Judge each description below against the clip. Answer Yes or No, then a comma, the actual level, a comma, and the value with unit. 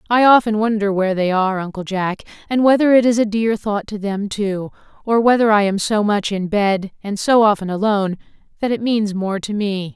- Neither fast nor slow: No, fast, 215 wpm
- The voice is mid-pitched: No, high, 205 Hz